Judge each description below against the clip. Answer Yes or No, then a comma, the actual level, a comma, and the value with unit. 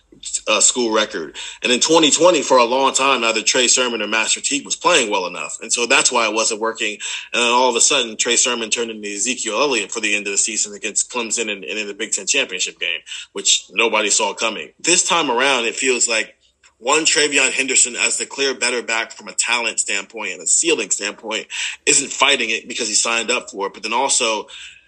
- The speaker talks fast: Yes, fast, 225 wpm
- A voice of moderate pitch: No, low, 125 Hz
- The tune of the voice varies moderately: No, wide, 6.5 semitones